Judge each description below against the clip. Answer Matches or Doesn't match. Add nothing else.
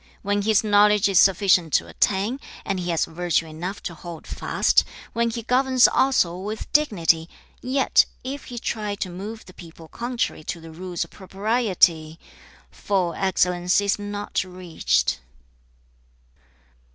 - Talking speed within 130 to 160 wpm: Matches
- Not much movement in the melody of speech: Doesn't match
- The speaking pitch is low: Doesn't match